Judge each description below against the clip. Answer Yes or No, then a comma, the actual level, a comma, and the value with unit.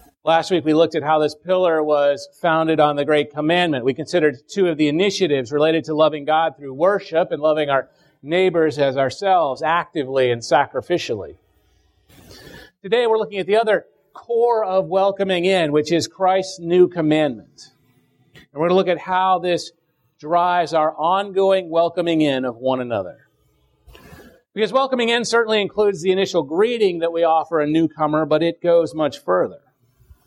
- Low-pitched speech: No, medium, 165 Hz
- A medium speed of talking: Yes, average, 165 wpm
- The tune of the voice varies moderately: Yes, average, 3.7 semitones